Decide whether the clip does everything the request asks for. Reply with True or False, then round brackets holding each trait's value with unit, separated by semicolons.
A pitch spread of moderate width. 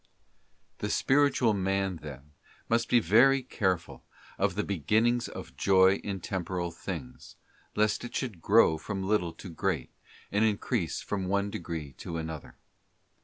True (4.1 semitones)